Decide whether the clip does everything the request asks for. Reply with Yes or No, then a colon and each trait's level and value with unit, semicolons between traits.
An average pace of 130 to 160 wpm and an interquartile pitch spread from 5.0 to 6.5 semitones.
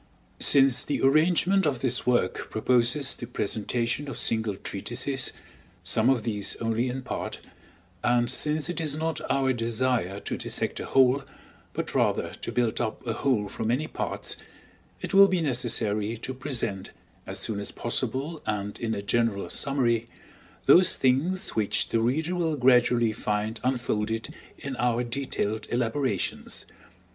No: average, 150 wpm; average, 3.6 semitones